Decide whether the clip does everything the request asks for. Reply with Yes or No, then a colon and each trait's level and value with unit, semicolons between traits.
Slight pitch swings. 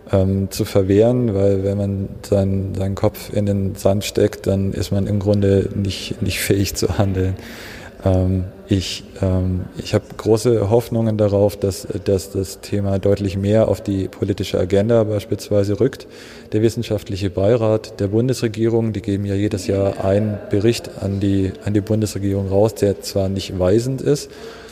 Yes: narrow, 1.8 semitones